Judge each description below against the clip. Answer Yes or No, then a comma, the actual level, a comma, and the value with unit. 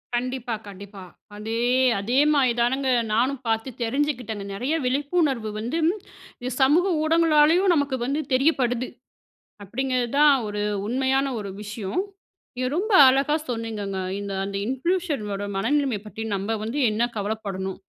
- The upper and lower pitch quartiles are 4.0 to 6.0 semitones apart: Yes, average, 4.9 semitones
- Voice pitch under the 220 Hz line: No, very high, 250 Hz